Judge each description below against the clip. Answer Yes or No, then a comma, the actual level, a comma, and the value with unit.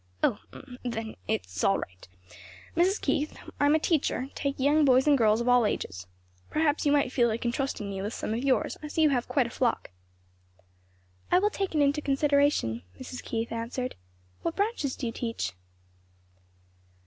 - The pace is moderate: Yes, average, 175 wpm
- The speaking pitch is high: Yes, very high, 260 Hz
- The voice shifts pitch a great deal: No, average, 4.4 semitones